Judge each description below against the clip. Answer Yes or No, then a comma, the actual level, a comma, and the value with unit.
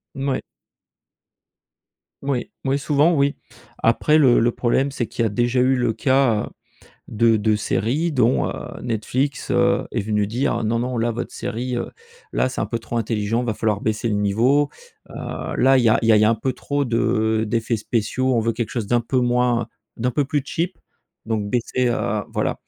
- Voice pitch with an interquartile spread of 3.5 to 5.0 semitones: No, average, 2.9 semitones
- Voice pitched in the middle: No, low, 120 Hz